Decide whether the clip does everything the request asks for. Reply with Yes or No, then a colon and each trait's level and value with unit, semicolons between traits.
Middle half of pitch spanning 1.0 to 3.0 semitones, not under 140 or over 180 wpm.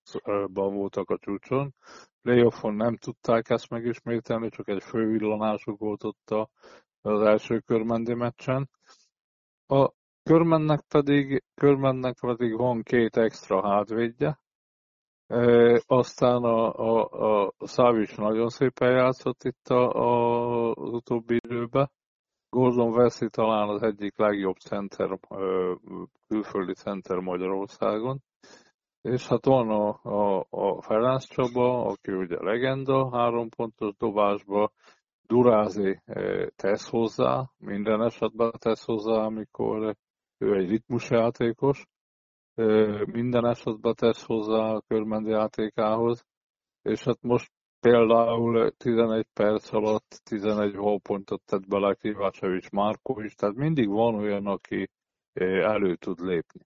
No: narrow, 2.6 semitones; average, 115 wpm